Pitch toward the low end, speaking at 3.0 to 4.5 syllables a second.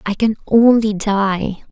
No: high, 210 Hz; 3.6 syllables/s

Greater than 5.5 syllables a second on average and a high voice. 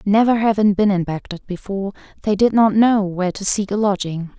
Yes: 5.7 syllables/s; high, 200 Hz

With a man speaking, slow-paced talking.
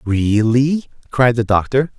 Yes: male; slow, 120 wpm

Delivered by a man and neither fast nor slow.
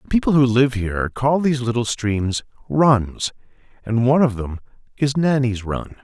Yes: male; average, 170 wpm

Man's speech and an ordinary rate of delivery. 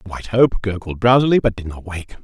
No: male; fast, 240 wpm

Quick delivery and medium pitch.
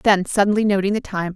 No: fast, 220 wpm; high, 200 Hz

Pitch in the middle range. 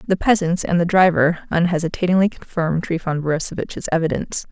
Yes: medium, 170 Hz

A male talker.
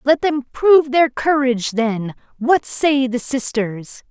No: female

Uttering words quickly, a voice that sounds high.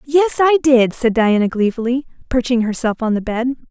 No: average, 180 wpm; very high, 250 Hz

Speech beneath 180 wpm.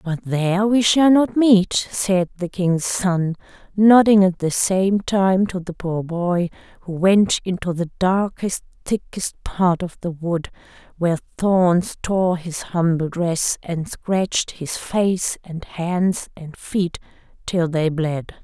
Yes: average, 150 wpm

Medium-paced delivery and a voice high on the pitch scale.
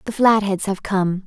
Yes: average, 190 wpm; high, 200 Hz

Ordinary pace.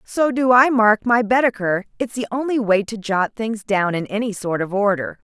No: fast, 215 wpm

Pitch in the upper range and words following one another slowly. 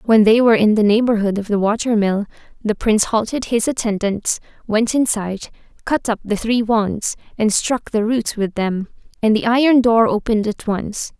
No: high, 220 Hz; average, 190 wpm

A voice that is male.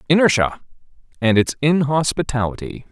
Yes: male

